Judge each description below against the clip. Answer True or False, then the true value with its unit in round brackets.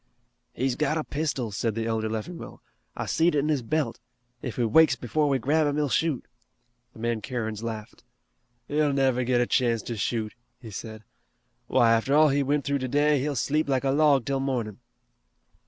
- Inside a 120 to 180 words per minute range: False (190 wpm)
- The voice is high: False (130 Hz)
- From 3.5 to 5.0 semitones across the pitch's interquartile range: True (4.2 semitones)